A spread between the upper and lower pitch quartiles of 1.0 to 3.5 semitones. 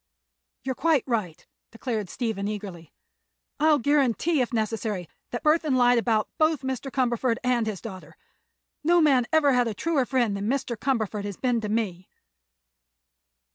No: average, 4.2 semitones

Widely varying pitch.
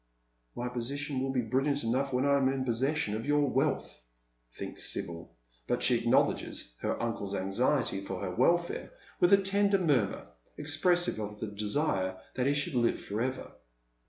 Yes: wide, 5.7 semitones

